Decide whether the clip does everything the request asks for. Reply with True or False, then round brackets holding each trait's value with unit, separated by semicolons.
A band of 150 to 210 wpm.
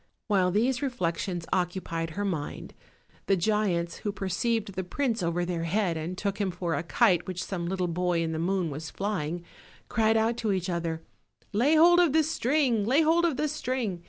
True (195 wpm)